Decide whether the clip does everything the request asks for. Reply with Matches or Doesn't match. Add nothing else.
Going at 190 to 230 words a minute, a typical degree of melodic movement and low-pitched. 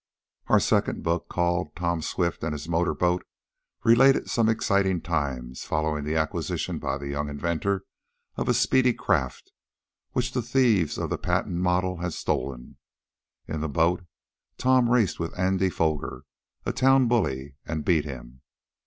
Doesn't match